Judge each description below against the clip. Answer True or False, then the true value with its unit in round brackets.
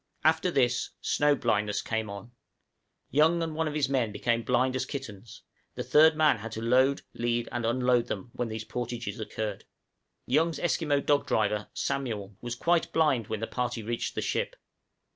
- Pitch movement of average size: True (4.5 semitones)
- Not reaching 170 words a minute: False (180 wpm)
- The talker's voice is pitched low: True (120 Hz)